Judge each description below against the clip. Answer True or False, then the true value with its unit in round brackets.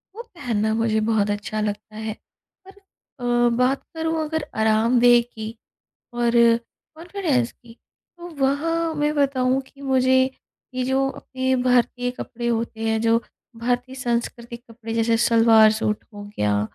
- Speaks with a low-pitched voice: False (240 Hz)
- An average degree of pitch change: True (3.1 semitones)